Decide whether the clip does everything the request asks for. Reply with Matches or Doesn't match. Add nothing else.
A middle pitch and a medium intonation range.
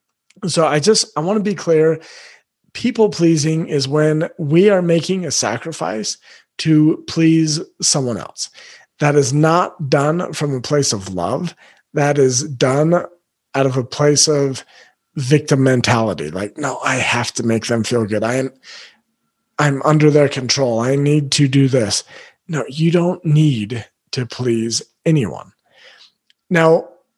Matches